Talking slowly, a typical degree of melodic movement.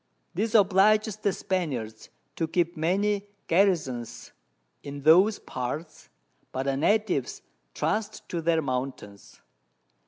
No: slow, 105 wpm; wide, 6.8 semitones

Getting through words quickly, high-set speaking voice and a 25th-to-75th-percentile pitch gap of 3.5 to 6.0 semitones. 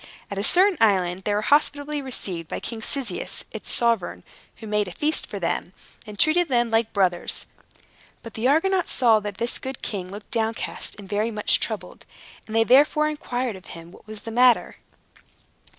No: average, 180 wpm; high, 225 Hz; average, 4.6 semitones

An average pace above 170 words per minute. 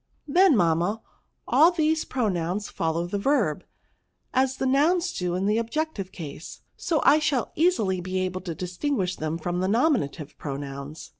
No: average, 160 wpm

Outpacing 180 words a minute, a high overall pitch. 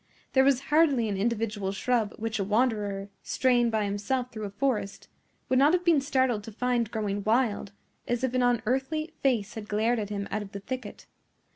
Yes: average, 190 wpm; high, 230 Hz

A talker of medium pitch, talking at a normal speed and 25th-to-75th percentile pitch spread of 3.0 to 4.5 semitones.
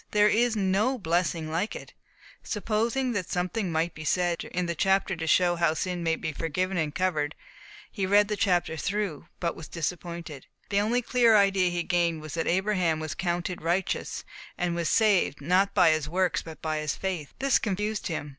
Yes: medium, 180 Hz; average, 190 wpm; average, 3.6 semitones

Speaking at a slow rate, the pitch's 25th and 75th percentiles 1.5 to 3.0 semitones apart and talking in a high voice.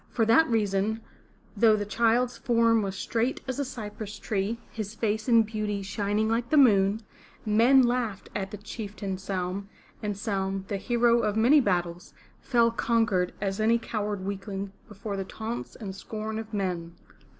No: average, 160 wpm; average, 2.7 semitones; high, 215 Hz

